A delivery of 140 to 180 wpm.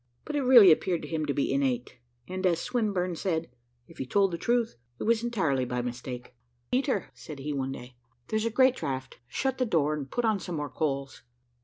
No: fast, 205 wpm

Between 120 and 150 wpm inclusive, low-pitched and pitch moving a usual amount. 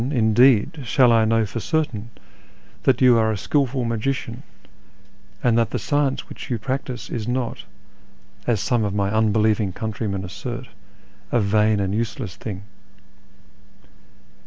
Yes: average, 140 wpm; low, 115 Hz; average, 3.0 semitones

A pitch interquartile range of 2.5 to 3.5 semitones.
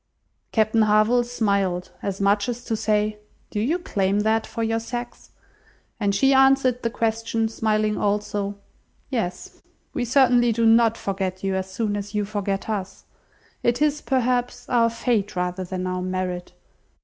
Yes: average, 3.0 semitones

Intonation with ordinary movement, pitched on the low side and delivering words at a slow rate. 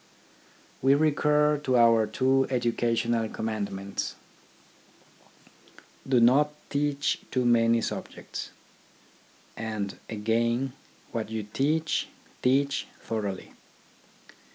Yes: average, 3.7 semitones; low, 120 Hz; slow, 90 wpm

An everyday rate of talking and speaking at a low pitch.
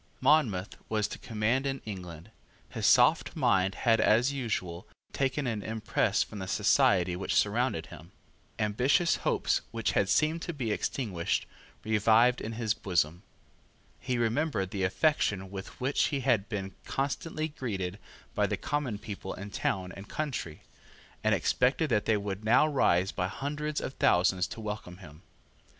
Yes: average, 155 wpm; low, 110 Hz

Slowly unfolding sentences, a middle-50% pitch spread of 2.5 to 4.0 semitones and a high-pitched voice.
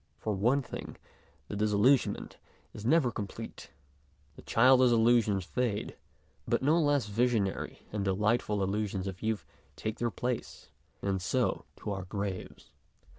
No: slow, 130 wpm; average, 3.6 semitones; low, 110 Hz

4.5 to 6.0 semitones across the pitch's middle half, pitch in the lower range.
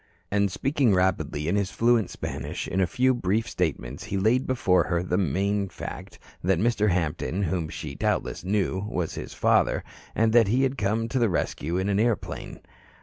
No: average, 4.1 semitones; low, 100 Hz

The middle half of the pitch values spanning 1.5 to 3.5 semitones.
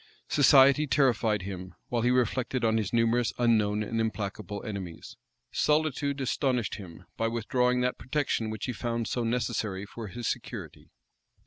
Yes: average, 3.0 semitones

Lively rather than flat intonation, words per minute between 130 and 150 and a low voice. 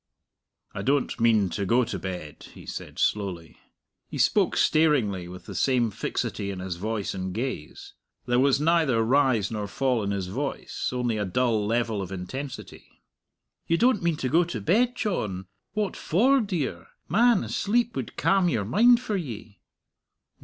No: wide, 8.7 semitones; average, 165 wpm; low, 120 Hz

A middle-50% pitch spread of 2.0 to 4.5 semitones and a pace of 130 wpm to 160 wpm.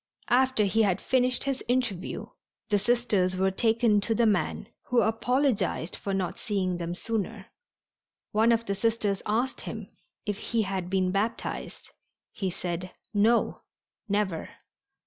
Yes: average, 3.4 semitones; average, 140 wpm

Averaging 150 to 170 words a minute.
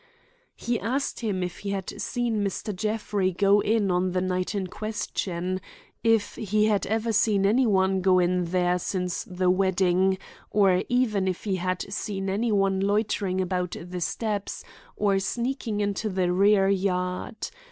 Yes: average, 160 wpm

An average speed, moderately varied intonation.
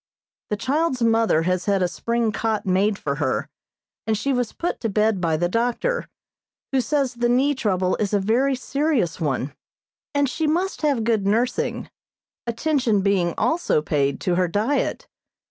No: average, 165 wpm; wide, 6.2 semitones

